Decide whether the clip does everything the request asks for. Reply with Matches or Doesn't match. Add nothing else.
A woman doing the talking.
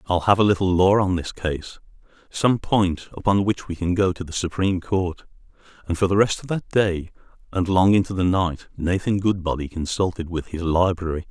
Doesn't match